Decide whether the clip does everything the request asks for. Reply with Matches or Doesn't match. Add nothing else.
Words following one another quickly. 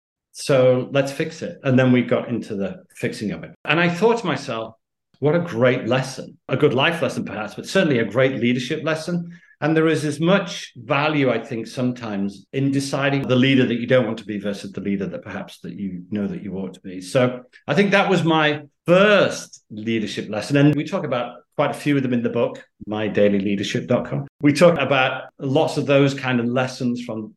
Matches